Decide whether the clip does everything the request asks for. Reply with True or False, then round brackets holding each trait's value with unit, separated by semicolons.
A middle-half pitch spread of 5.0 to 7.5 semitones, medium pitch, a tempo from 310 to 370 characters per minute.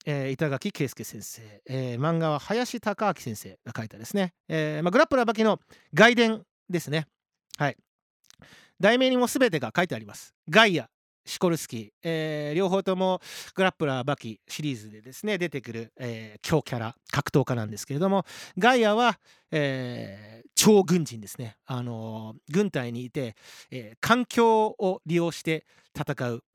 False (8.0 semitones; 155 Hz; 320 characters per minute)